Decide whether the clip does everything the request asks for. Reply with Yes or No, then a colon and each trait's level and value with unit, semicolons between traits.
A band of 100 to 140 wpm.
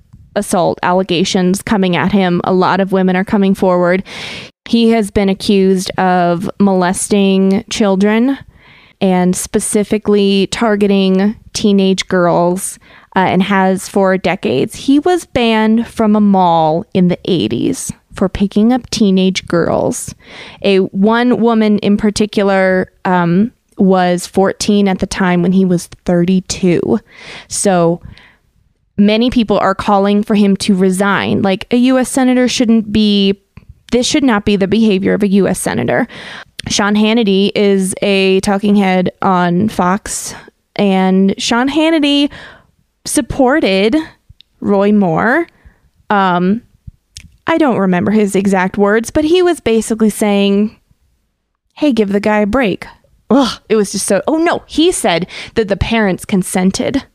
Yes: slow, 135 wpm